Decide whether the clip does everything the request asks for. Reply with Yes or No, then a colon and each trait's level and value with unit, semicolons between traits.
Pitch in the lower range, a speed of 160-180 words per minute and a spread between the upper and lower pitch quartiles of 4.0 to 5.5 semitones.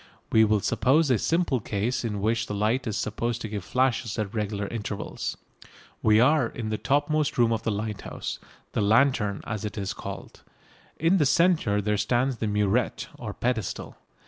No: low, 110 Hz; average, 175 wpm; average, 3.6 semitones